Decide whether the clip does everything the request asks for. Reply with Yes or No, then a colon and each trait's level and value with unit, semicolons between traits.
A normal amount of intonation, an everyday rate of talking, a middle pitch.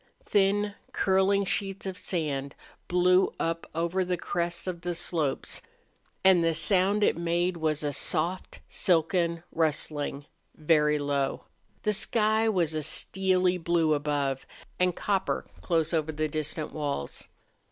No: average, 3.2 semitones; slow, 130 wpm; medium, 170 Hz